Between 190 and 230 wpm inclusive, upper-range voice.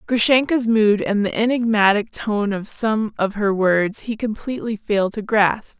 No: average, 165 wpm; high, 215 Hz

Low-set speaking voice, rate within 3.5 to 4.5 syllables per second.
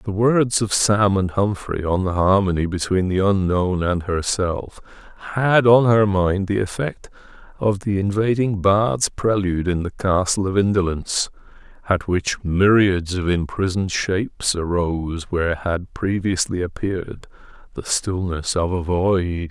Yes: very low, 95 Hz; 4.3 syllables/s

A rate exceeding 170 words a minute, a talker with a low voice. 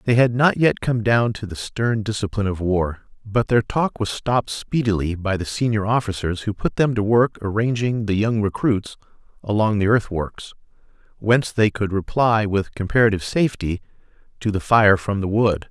Yes: average, 180 wpm; low, 105 Hz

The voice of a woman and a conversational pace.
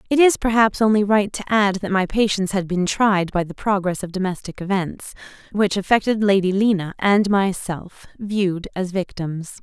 Yes: female; average, 170 wpm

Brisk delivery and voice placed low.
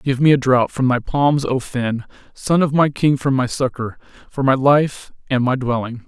Yes: fast, 215 wpm; low, 130 Hz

